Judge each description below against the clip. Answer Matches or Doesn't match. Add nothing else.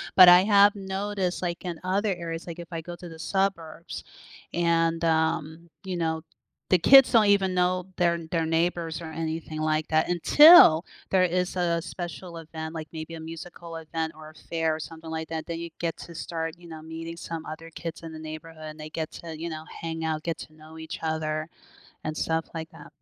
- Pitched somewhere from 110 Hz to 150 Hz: Doesn't match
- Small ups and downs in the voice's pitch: Matches